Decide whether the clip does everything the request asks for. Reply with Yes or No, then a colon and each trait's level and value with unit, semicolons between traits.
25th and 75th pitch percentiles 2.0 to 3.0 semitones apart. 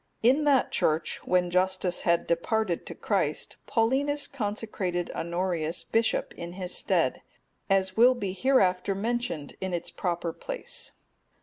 No: average, 4.9 semitones